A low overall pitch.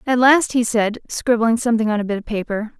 No: high, 230 Hz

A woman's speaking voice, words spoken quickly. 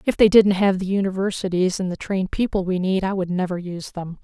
Yes: female; fast, 240 wpm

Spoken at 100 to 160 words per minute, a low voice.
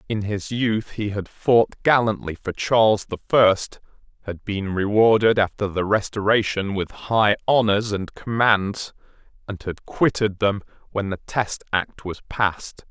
Yes: average, 150 wpm; low, 105 Hz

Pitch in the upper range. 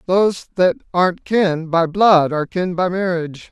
No: medium, 175 Hz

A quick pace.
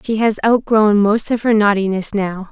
No: average, 190 wpm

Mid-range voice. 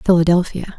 Yes: medium, 175 Hz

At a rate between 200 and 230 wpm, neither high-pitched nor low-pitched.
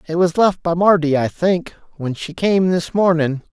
Yes: fast, 205 wpm; medium, 170 Hz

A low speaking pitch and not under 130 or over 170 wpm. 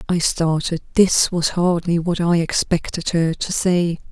No: medium, 170 Hz; average, 160 wpm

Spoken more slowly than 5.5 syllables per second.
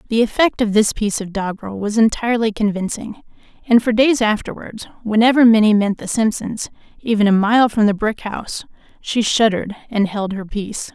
No: 5.6 syllables/s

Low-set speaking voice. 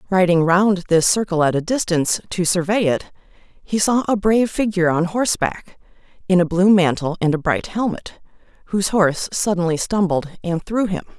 No: medium, 185 Hz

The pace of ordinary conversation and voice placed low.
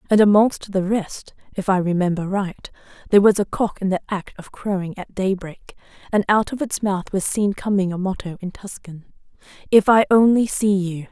No: average, 195 wpm; high, 195 Hz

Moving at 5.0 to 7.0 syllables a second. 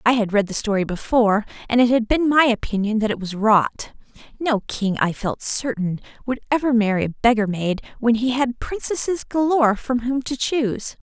Yes: 5.2 syllables/s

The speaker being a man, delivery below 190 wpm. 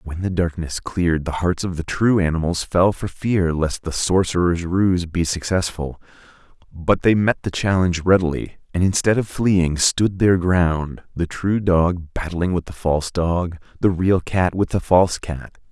Yes: male; average, 180 wpm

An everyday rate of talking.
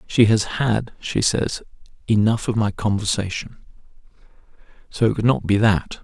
Yes: average, 150 wpm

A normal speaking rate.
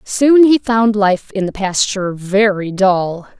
Yes: average, 160 wpm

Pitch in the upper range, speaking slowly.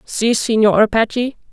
Yes: high, 225 Hz; slow, 120 wpm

